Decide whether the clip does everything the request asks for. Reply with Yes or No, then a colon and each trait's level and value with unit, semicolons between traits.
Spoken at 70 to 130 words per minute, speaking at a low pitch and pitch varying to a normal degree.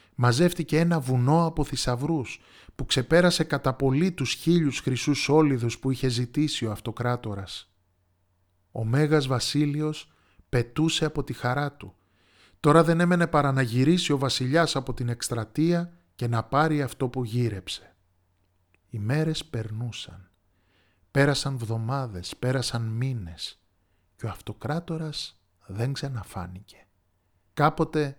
No: average, 120 wpm; low, 125 Hz; wide, 7.0 semitones